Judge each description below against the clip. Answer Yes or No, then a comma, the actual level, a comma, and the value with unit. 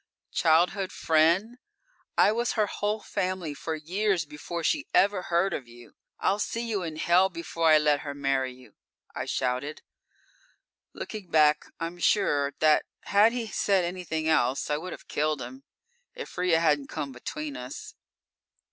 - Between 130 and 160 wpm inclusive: Yes, average, 155 wpm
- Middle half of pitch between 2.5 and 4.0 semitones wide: No, average, 4.8 semitones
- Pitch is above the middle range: No, medium, 165 Hz